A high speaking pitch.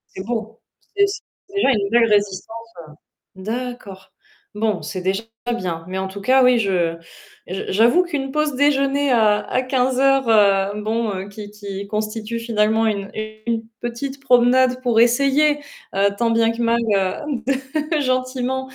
Yes: high, 230 Hz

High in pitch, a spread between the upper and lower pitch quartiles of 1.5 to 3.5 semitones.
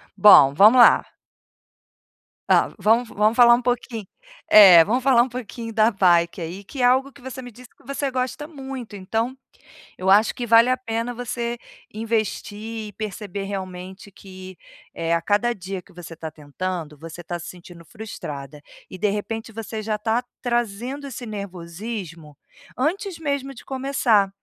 No: high, 215 Hz; average, 4.7 semitones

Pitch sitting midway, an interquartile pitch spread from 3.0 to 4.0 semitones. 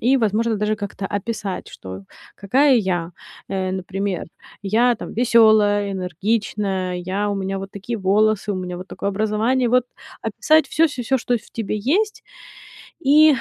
No: high, 210 Hz; average, 3.5 semitones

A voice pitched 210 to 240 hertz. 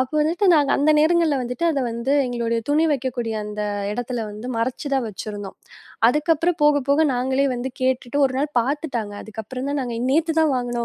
No: very high, 260 Hz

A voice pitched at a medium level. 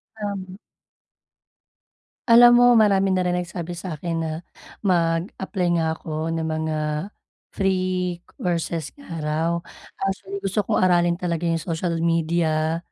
Yes: medium, 175 Hz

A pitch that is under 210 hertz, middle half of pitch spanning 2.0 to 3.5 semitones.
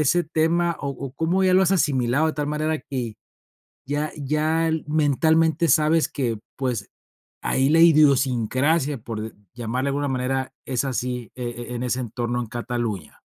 No: medium, 140 Hz; average, 4.2 semitones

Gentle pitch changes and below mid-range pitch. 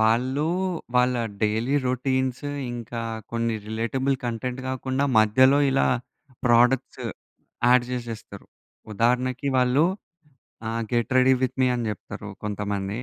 Yes: narrow, 2.3 semitones; low, 125 Hz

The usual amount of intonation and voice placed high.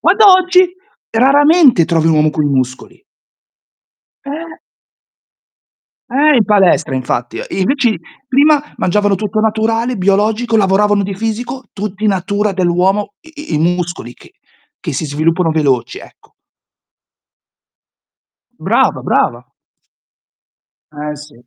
No: wide, 7.1 semitones; high, 205 Hz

